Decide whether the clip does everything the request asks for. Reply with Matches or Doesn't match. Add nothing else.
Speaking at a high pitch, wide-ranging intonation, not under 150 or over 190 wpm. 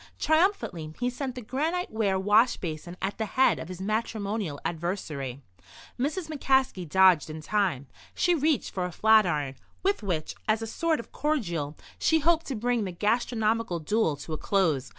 Matches